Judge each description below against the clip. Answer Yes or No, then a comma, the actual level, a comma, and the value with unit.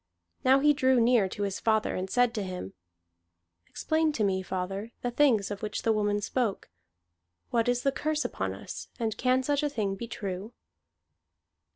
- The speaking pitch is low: No, high, 225 Hz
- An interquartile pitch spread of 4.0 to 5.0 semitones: Yes, average, 4.5 semitones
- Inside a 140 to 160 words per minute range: No, average, 180 wpm